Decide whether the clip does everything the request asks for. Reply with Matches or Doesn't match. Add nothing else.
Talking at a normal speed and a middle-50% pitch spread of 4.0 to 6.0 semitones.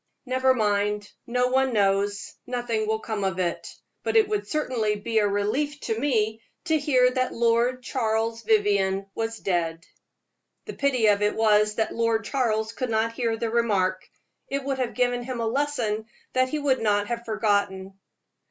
Doesn't match